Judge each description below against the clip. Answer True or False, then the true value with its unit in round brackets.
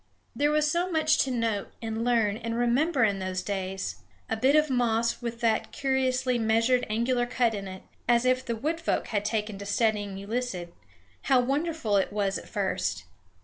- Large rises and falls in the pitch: False (3.8 semitones)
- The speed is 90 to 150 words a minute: False (185 wpm)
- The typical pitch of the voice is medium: False (230 Hz)